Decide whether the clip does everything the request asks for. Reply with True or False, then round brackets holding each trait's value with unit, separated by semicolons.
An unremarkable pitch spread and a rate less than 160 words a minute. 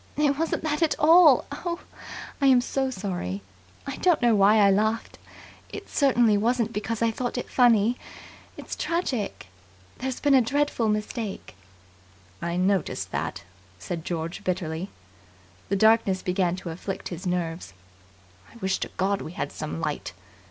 False (5.8 semitones; 150 wpm)